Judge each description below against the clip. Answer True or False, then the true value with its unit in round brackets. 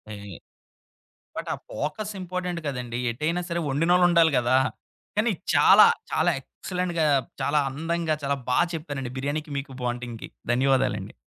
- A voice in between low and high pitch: True (150 Hz)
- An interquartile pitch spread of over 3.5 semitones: True (4.8 semitones)